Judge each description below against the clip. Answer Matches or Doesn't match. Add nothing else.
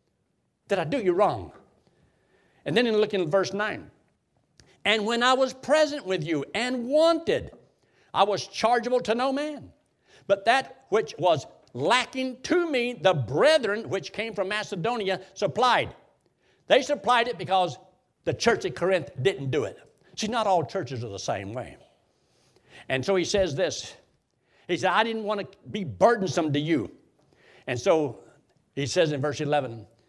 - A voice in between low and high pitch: Doesn't match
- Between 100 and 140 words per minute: Doesn't match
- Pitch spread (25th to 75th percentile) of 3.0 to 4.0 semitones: Doesn't match